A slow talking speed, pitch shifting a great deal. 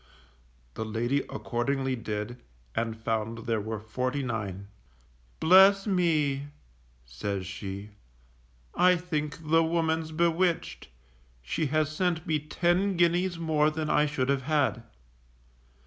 Yes: slow, 120 wpm; wide, 6.6 semitones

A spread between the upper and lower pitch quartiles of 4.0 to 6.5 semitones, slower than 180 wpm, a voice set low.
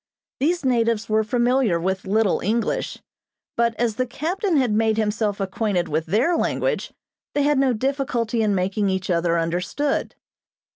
No: average, 4.9 semitones; average, 150 wpm; high, 225 Hz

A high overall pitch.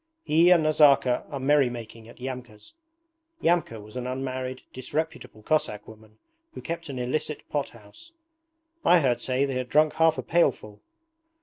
No: low, 130 Hz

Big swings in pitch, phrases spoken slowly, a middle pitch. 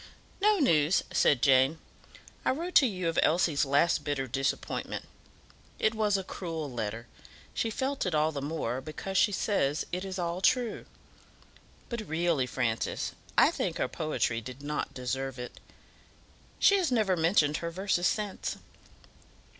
No: wide, 6.5 semitones; average, 150 wpm; medium, 165 Hz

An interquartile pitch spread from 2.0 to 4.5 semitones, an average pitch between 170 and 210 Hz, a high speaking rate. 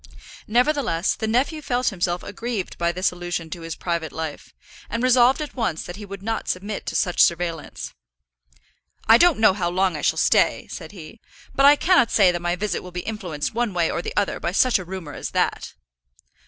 No: average, 4.9 semitones; high, 190 Hz; fast, 210 wpm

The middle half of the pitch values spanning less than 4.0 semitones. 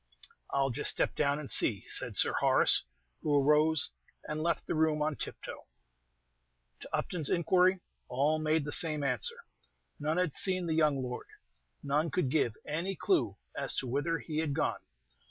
Yes: narrow, 2.5 semitones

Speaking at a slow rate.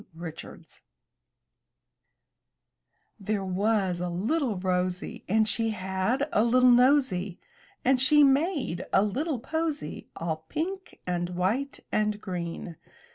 Yes: slow, 110 wpm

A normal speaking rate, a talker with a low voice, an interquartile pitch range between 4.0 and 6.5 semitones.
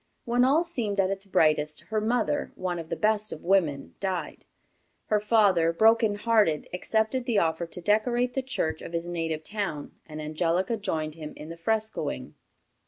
No: average, 170 wpm; high, 195 Hz; average, 5.1 semitones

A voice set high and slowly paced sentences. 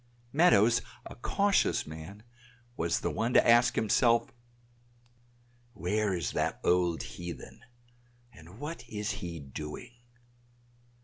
No: low, 105 Hz; slow, 110 wpm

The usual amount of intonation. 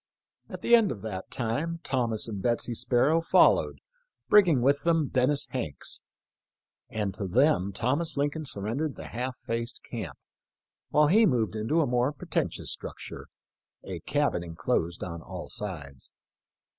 No: wide, 6.2 semitones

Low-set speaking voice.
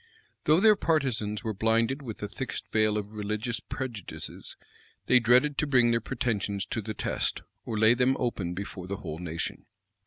Yes: low, 115 Hz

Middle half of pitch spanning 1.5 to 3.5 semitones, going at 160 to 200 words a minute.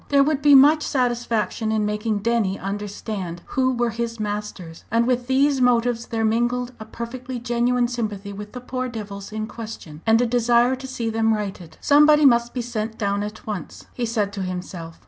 Yes: average, 2.9 semitones; average, 185 wpm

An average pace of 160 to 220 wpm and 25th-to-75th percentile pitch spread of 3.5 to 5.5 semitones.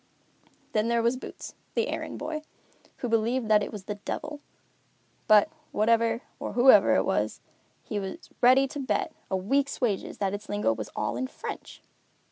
Yes: average, 170 wpm; average, 4.0 semitones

